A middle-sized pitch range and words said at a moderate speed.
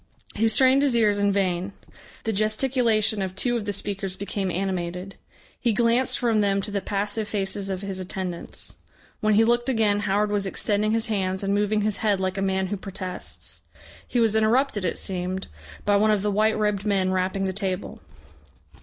No: narrow, 2.1 semitones; average, 190 wpm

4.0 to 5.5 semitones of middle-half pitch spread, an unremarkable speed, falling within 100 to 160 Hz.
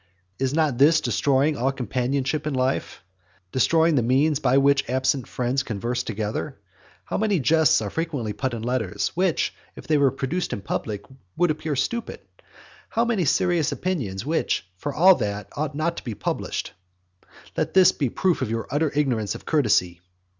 Yes: average, 4.8 semitones; average, 175 wpm; low, 135 Hz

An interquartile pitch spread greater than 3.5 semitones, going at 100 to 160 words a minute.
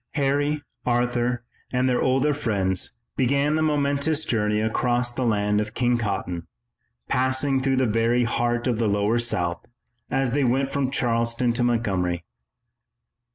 No: average, 3.2 semitones; average, 145 wpm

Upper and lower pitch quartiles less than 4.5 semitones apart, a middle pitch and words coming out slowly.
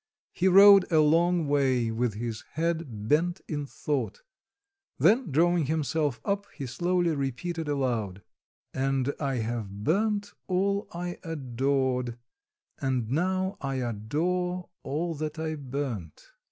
No: wide, 5.5 semitones; medium, 150 Hz; slow, 125 wpm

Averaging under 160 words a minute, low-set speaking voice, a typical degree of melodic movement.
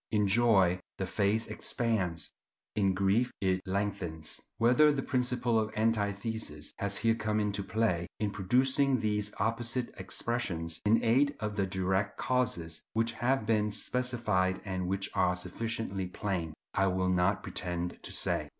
Yes: average, 145 wpm; low, 105 Hz; average, 3.6 semitones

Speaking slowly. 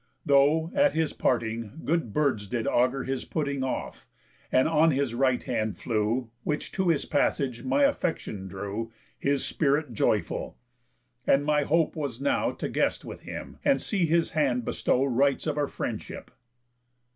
No: average, 155 wpm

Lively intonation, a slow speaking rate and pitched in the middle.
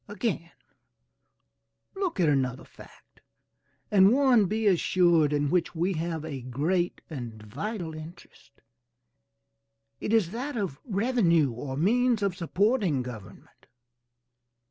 Yes: wide, 6.2 semitones; slow, 115 wpm; medium, 175 Hz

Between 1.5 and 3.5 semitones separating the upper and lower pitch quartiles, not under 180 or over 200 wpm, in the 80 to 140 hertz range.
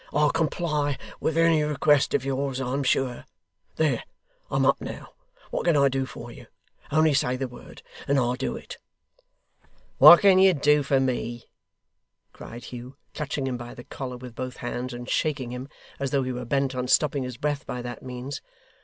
Yes: average, 2.8 semitones; average, 185 wpm; low, 135 Hz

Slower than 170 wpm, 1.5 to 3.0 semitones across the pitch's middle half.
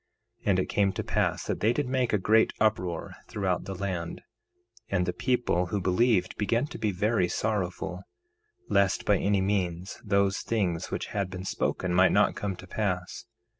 No: average, 180 wpm; narrow, 2.6 semitones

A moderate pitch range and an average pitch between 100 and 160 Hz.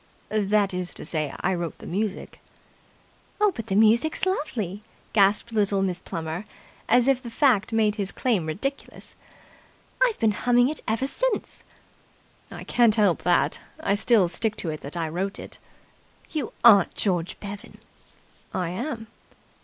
No: average, 4.6 semitones; high, 210 Hz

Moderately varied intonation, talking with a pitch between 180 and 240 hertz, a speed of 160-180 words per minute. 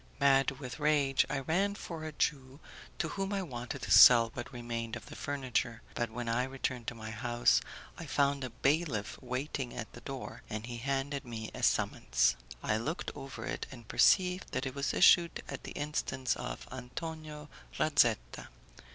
No: average, 3.9 semitones; low, 135 Hz; average, 175 wpm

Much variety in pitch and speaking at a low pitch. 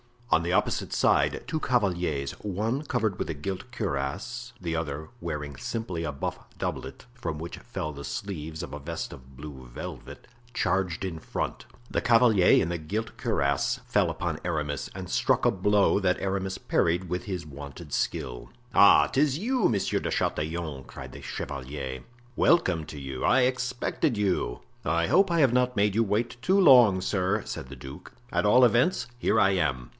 Yes: wide, 7.2 semitones; very low, 90 Hz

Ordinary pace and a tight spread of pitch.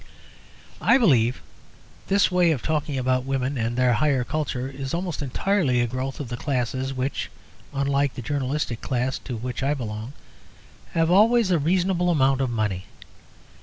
No: average, 160 wpm; average, 3.8 semitones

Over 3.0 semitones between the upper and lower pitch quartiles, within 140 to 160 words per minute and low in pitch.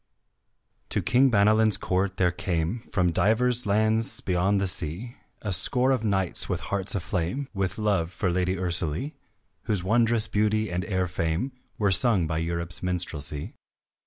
Yes: average, 3.7 semitones; average, 150 wpm; very low, 95 Hz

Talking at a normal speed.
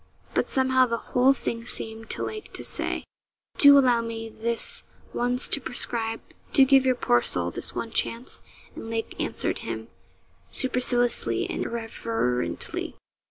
Yes: average, 145 wpm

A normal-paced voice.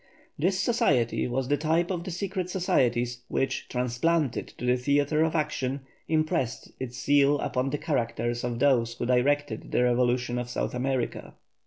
Yes: average, 160 wpm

